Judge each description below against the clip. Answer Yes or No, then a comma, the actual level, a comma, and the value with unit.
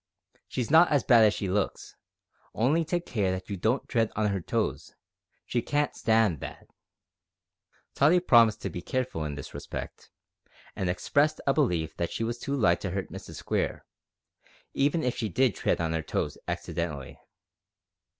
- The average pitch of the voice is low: Yes, low, 110 Hz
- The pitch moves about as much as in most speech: No, wide, 7.4 semitones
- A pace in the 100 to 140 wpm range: No, average, 170 wpm